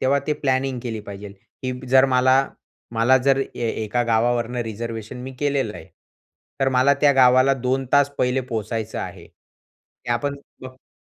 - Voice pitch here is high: No, low, 125 Hz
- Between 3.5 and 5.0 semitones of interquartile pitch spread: No, narrow, 2.6 semitones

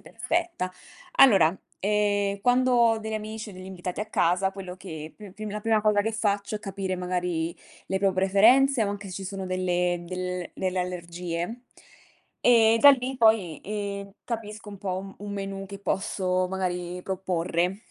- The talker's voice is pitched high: Yes, high, 195 Hz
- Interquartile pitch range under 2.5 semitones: No, average, 2.8 semitones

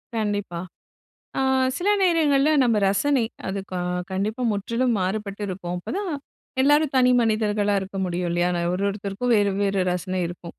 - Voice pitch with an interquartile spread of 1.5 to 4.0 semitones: No, average, 4.8 semitones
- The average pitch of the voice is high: Yes, high, 205 Hz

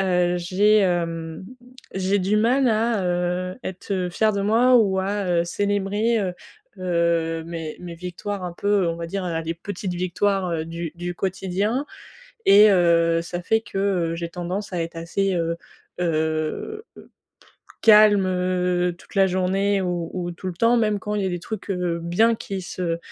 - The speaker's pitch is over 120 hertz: Yes, medium, 185 Hz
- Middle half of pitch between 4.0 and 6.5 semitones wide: No, average, 2.9 semitones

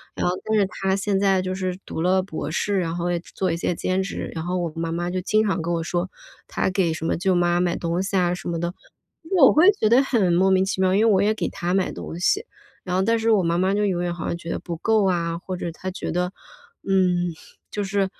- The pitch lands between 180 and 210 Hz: Yes, medium, 185 Hz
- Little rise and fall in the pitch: Yes, narrow, 2.0 semitones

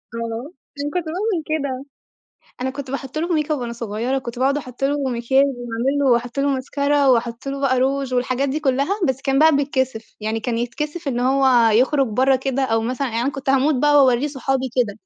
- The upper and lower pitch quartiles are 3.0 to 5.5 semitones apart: No, narrow, 2.5 semitones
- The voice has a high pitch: Yes, very high, 265 Hz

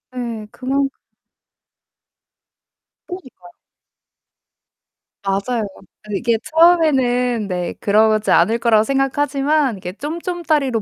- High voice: Yes, very high, 250 Hz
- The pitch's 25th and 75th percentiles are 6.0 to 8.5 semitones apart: No, average, 5.1 semitones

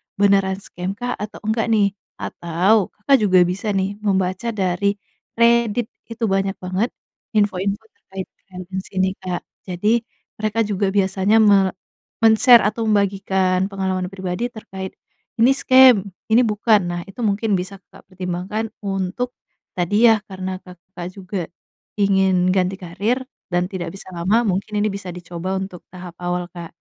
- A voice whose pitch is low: No, high, 195 Hz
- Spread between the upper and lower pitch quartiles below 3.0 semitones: Yes, narrow, 2.5 semitones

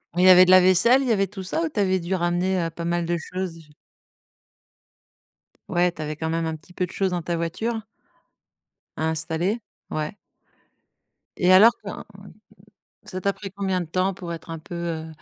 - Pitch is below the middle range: No, medium, 180 Hz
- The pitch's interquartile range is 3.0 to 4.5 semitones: No, narrow, 2.4 semitones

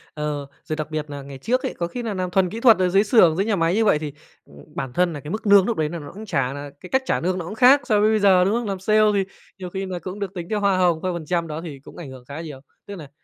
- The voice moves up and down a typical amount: Yes, average, 4.9 semitones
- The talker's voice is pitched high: No, medium, 180 Hz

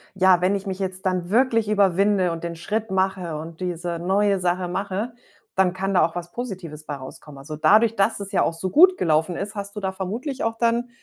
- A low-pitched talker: No, high, 190 Hz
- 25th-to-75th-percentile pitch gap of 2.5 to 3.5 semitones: Yes, average, 2.9 semitones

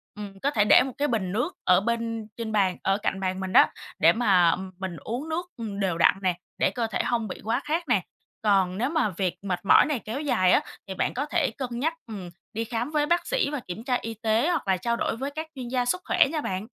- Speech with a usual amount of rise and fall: No, wide, 6.1 semitones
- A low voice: No, high, 225 Hz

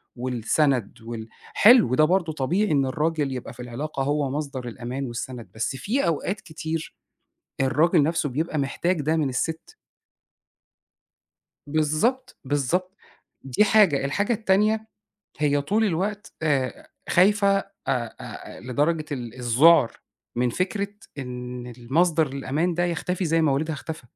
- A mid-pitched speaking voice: Yes, medium, 150 Hz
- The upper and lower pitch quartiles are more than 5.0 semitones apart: Yes, wide, 5.4 semitones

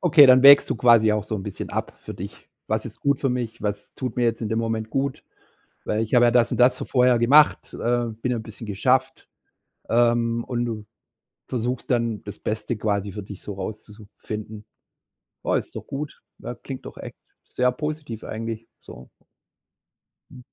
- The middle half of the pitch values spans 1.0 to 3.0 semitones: Yes, average, 2.7 semitones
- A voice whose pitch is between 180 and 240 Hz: No, low, 115 Hz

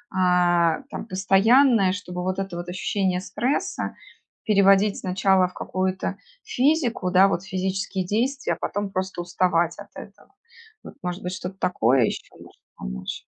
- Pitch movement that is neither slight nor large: No, narrow, 1.9 semitones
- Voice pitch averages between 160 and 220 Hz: Yes, high, 190 Hz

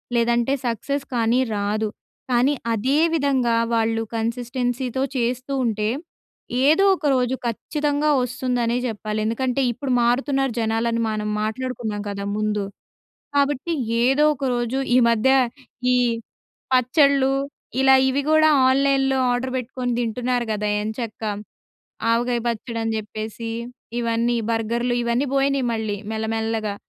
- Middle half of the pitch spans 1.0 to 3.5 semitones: Yes, average, 2.9 semitones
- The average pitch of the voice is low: No, high, 240 Hz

